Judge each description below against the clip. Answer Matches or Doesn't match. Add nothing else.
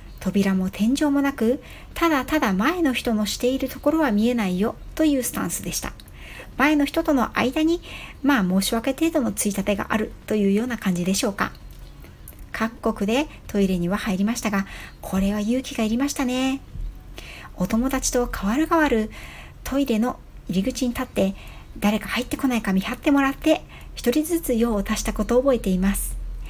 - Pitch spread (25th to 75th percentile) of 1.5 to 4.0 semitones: Doesn't match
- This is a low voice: Doesn't match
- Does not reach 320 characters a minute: Doesn't match